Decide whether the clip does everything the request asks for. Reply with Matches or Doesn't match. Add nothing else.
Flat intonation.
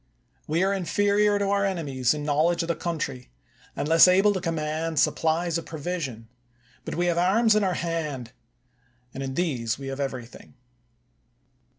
Doesn't match